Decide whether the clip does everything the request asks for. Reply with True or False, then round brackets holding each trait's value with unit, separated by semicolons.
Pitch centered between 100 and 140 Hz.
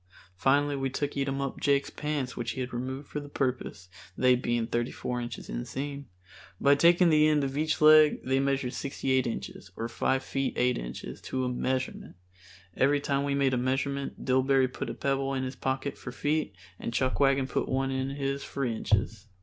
True (135 Hz)